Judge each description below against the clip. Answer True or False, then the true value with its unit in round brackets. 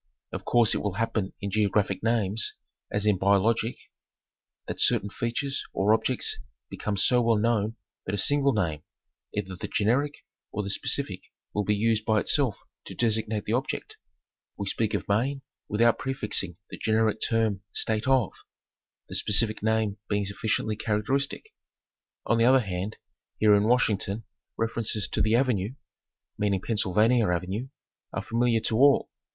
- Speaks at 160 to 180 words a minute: False (150 wpm)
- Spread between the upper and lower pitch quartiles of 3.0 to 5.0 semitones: False (2.4 semitones)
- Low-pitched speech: True (110 Hz)